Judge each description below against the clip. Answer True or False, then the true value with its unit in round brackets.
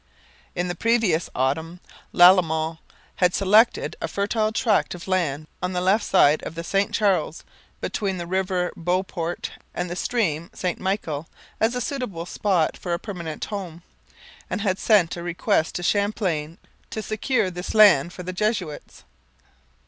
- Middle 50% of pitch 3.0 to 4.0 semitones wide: True (3.4 semitones)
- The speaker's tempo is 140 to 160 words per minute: True (155 wpm)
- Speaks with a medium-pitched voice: True (180 Hz)